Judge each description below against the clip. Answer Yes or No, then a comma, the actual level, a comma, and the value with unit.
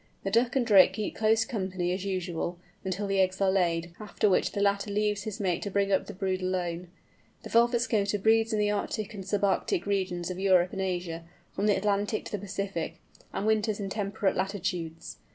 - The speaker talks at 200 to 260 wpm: Yes, fast, 205 wpm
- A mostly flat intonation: Yes, narrow, 2.2 semitones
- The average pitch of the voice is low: No, high, 195 Hz